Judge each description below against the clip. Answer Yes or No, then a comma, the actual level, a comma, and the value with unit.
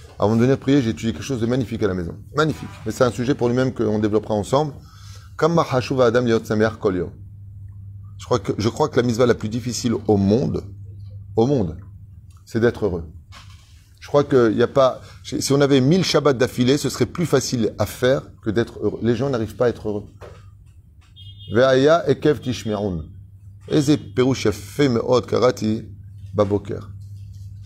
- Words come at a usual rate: Yes, average, 165 wpm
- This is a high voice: No, low, 110 Hz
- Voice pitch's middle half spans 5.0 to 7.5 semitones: No, average, 4.2 semitones